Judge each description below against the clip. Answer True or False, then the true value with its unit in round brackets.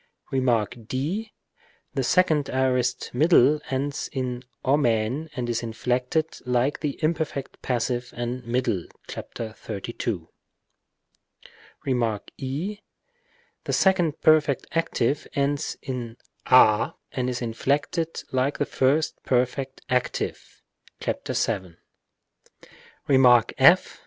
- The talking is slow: True (100 wpm)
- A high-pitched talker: False (130 Hz)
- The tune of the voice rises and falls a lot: False (3.2 semitones)